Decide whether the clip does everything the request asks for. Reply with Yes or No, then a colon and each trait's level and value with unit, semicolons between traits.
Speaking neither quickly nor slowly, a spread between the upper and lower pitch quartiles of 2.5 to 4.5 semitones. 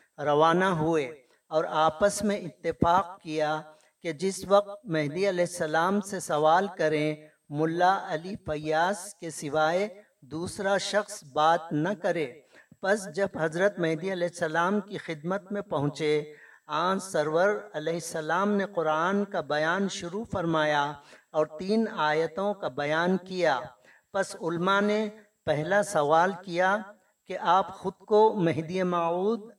Yes: average, 130 wpm; average, 4.1 semitones